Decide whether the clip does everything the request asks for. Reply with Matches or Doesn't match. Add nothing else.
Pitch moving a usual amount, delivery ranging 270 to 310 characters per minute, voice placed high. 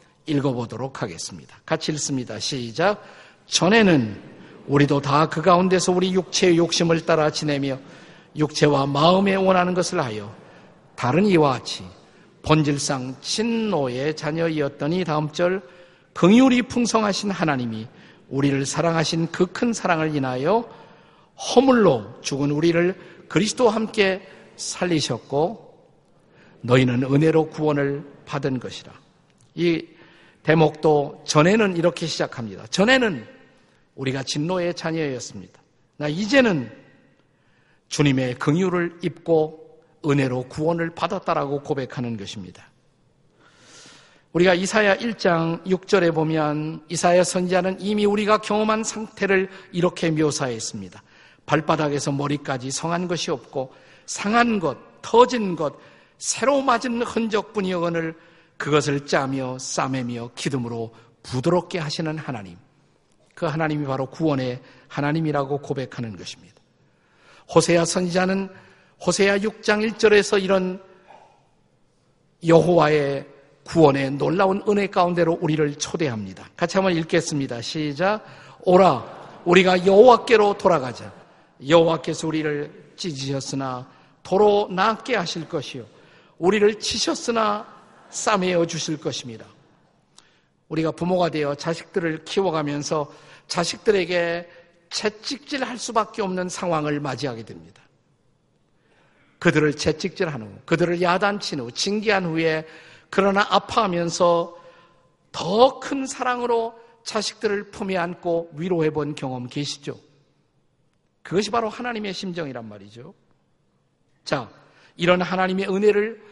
Doesn't match